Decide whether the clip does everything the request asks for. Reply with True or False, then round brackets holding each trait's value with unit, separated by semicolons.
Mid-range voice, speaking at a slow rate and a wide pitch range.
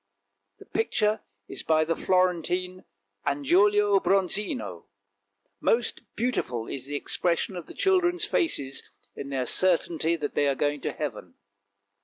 True (170 Hz; 130 wpm; 6.1 semitones)